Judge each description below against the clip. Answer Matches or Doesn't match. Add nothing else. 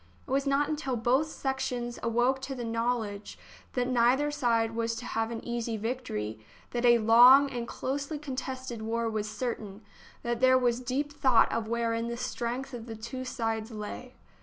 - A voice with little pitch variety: Matches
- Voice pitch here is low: Doesn't match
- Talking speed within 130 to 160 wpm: Doesn't match